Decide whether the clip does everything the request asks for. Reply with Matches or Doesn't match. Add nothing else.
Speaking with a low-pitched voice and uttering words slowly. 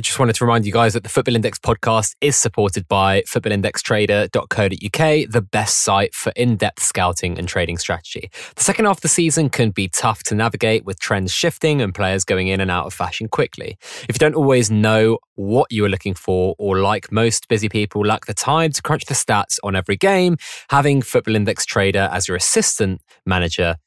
Doesn't match